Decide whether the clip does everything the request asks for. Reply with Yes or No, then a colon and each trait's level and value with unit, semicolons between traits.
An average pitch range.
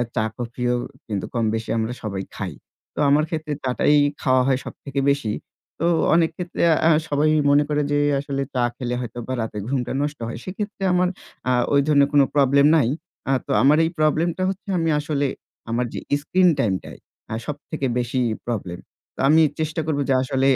Yes: average, 3.9 semitones